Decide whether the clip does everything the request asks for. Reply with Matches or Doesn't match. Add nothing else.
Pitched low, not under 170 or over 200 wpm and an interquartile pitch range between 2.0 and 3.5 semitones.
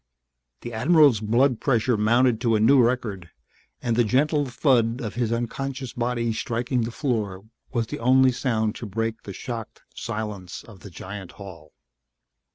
Doesn't match